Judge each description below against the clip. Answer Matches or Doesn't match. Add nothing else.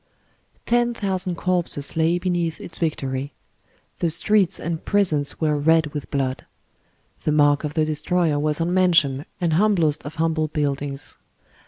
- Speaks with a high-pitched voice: Doesn't match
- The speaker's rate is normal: Matches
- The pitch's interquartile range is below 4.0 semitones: Matches